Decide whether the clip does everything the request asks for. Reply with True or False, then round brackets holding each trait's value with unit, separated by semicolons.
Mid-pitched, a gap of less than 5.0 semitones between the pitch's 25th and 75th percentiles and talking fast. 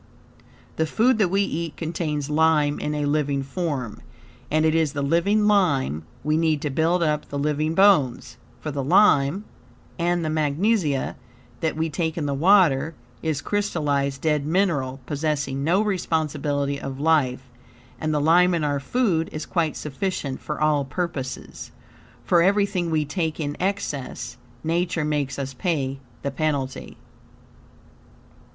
False (155 Hz; 3.3 semitones; 145 wpm)